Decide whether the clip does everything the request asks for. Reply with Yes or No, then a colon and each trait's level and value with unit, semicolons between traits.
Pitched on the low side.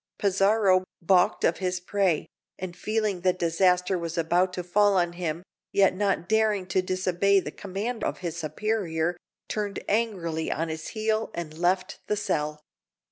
No: medium, 185 Hz